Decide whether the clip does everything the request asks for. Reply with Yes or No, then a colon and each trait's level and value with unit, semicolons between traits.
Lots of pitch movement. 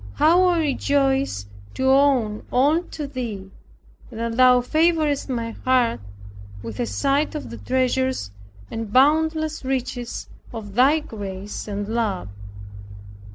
No: average, 4.5 semitones